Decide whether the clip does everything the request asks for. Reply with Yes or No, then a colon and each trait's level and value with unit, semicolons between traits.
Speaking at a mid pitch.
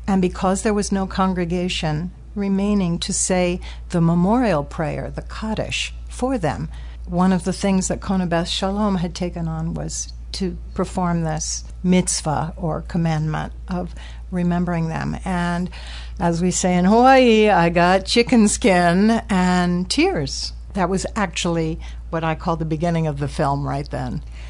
Yes: medium, 180 Hz